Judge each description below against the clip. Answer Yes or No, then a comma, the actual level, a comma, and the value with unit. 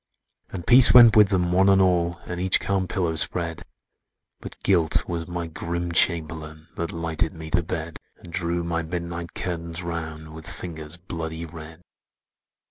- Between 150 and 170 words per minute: Yes, average, 160 wpm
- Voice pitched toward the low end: Yes, very low, 85 Hz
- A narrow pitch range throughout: Yes, narrow, 1.5 semitones